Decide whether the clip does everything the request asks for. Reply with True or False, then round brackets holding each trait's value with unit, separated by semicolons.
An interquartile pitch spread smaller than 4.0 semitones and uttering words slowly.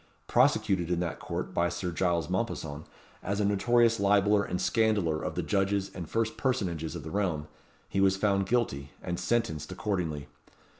False (3.5 semitones; 165 wpm)